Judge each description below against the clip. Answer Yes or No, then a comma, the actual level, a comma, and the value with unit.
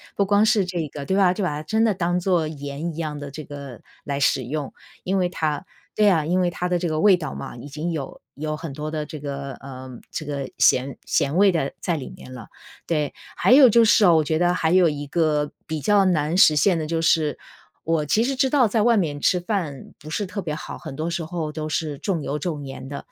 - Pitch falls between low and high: Yes, medium, 160 Hz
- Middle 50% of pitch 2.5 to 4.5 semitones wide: Yes, average, 3.8 semitones